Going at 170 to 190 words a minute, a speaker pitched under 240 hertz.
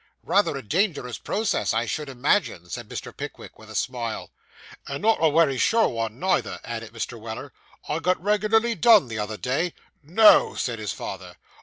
Yes: average, 175 wpm; medium, 140 Hz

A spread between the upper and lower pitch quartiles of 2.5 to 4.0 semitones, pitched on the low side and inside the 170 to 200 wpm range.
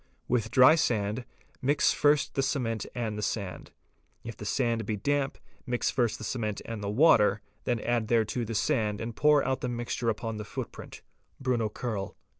Yes: average, 3.1 semitones; low, 115 Hz; average, 180 wpm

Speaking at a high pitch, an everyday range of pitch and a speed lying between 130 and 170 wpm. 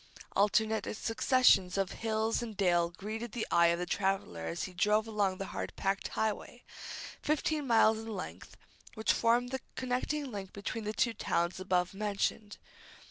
Yes: high, 210 Hz; average, 3.1 semitones; average, 160 wpm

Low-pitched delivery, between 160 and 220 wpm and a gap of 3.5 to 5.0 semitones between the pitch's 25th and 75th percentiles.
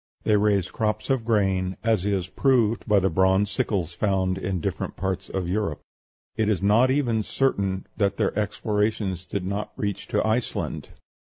No: low, 100 Hz; average, 165 wpm; narrow, 2.4 semitones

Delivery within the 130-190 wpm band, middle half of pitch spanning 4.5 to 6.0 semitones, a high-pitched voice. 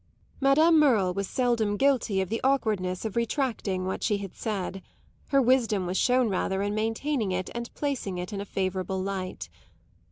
Yes: average, 170 wpm; average, 4.9 semitones; high, 210 Hz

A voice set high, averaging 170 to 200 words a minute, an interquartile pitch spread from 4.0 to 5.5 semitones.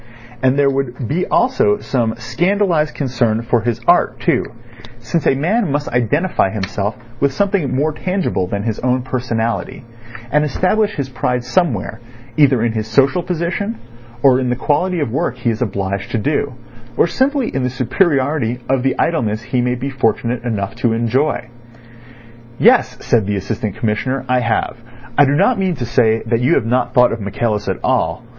No: low, 125 Hz; average, 180 wpm; average, 4.6 semitones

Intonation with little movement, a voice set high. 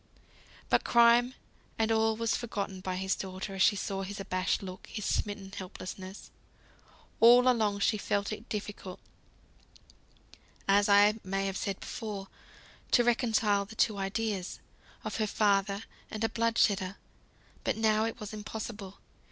Yes: narrow, 2.3 semitones; high, 205 Hz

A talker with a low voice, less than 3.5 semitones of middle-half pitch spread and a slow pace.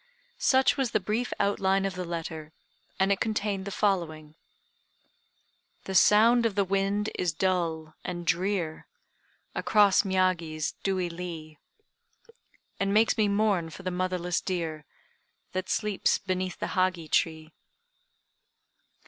No: medium, 185 Hz; average, 3.1 semitones; slow, 125 wpm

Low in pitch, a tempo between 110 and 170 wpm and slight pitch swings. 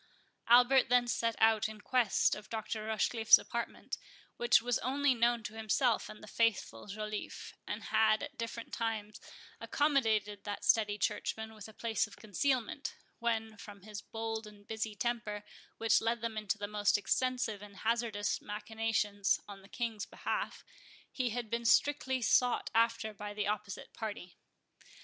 No: high, 220 Hz; average, 155 wpm; narrow, 2.0 semitones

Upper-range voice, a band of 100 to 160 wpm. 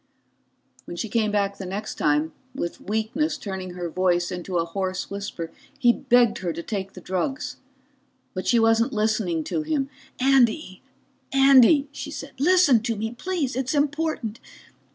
Yes: high, 220 Hz; average, 155 wpm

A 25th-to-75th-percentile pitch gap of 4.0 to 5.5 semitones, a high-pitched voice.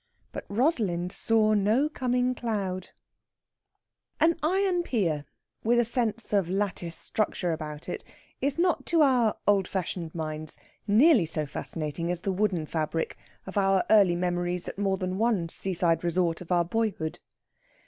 Yes: average, 5.1 semitones; high, 195 Hz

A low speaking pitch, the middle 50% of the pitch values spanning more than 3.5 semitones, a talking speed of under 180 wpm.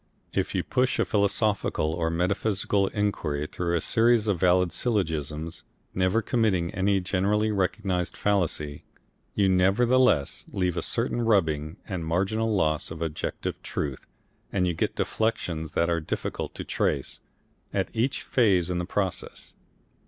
Yes: very low, 95 Hz; average, 3.9 semitones; average, 140 wpm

